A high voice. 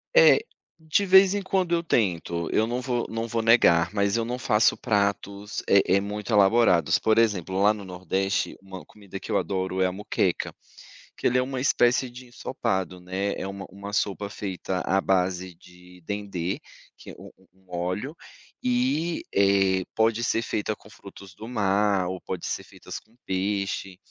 No: low, 100 Hz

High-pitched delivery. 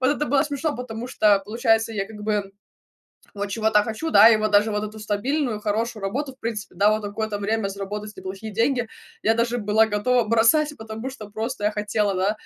Yes: high, 220 Hz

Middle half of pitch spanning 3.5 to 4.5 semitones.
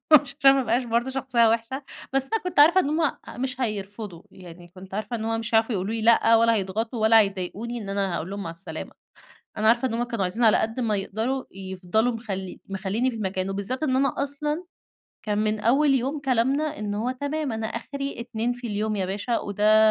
Yes: average, 4.2 semitones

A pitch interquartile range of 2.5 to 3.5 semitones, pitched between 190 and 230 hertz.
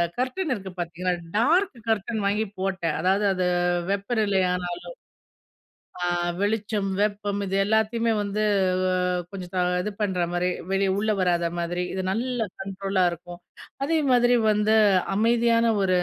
Yes: average, 3.2 semitones; high, 200 Hz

